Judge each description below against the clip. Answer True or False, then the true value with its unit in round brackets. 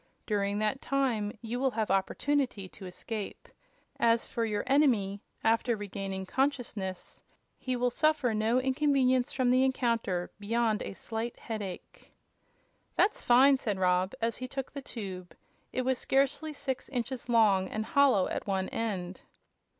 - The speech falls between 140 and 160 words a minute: True (145 wpm)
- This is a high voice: True (230 Hz)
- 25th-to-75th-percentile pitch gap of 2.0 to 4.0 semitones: False (4.4 semitones)